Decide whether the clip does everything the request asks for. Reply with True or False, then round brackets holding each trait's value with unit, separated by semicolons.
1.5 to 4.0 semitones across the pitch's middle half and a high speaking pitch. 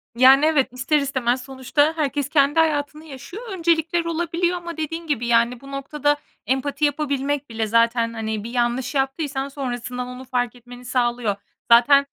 True (3.5 semitones; 270 Hz)